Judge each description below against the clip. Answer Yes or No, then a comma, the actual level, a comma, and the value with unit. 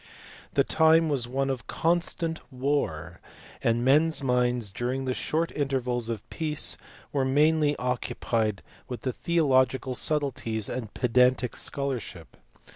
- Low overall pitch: Yes, low, 130 Hz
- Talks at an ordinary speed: No, slow, 125 wpm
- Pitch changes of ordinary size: Yes, average, 3.3 semitones